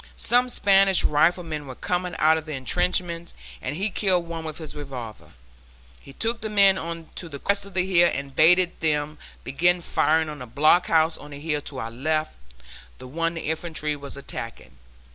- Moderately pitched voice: Yes, medium, 160 Hz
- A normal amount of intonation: Yes, average, 3.4 semitones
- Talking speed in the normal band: Yes, average, 185 wpm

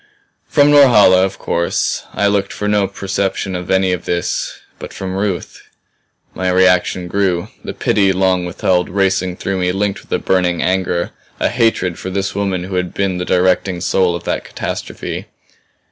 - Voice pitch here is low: Yes, very low, 95 Hz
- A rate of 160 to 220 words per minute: Yes, average, 170 wpm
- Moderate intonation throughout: No, narrow, 1.5 semitones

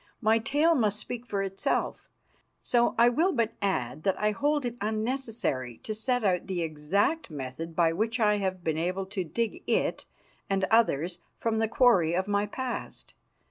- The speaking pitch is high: Yes, high, 210 Hz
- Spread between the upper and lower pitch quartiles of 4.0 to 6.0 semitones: Yes, average, 4.8 semitones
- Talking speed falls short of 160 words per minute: No, average, 175 wpm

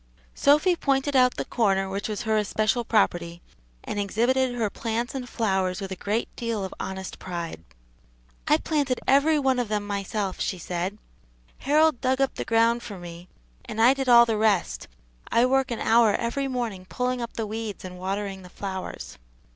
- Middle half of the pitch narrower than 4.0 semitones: No, average, 4.6 semitones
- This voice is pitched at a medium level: No, high, 225 Hz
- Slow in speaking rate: No, average, 180 wpm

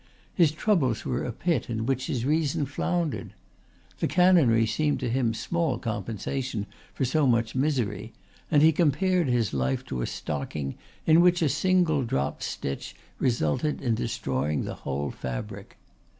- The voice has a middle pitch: No, low, 130 Hz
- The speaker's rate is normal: Yes, average, 150 wpm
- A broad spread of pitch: Yes, wide, 6.0 semitones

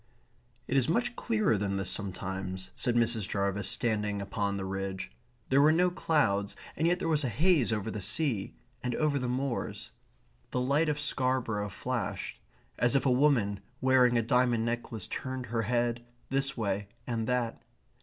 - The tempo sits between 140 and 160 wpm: No, average, 170 wpm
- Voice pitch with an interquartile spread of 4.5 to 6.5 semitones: Yes, average, 5.0 semitones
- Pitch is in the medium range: No, low, 120 Hz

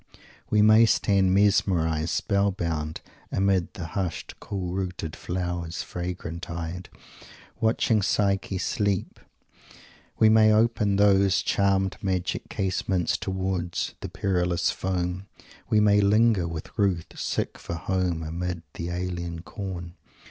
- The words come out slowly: Yes, slow, 120 wpm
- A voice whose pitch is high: No, very low, 95 Hz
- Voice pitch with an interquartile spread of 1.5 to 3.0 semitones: Yes, narrow, 2.4 semitones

